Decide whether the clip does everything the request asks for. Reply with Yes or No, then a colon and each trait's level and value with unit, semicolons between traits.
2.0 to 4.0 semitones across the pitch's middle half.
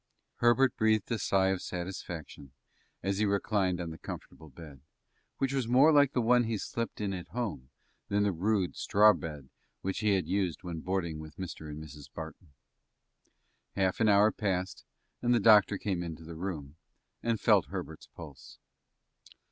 No: average, 4.8 semitones